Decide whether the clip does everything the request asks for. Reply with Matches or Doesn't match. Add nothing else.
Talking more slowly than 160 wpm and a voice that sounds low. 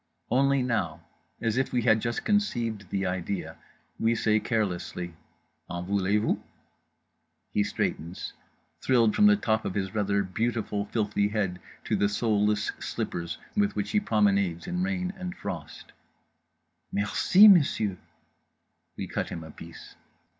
Matches